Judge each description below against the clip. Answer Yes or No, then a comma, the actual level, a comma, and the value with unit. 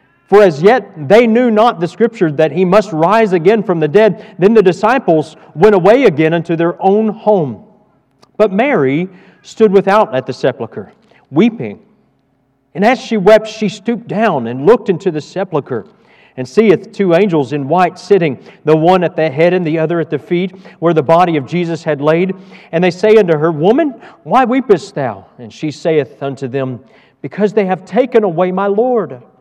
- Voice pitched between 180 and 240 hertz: Yes, medium, 185 Hz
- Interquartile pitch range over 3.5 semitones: Yes, average, 5.1 semitones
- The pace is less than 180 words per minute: No, average, 190 wpm